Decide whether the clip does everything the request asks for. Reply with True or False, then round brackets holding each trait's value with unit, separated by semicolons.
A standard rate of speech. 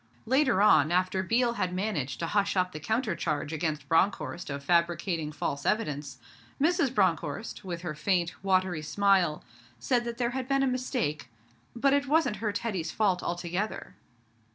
True (160 wpm)